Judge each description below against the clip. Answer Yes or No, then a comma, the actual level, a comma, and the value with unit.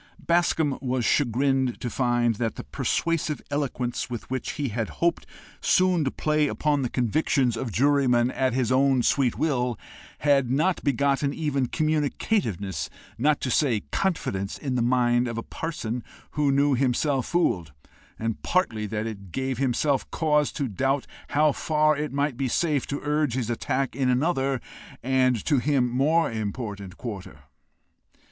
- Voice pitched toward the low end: Yes, low, 130 Hz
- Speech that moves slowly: No, average, 155 wpm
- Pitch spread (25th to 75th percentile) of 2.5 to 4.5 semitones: Yes, average, 3.5 semitones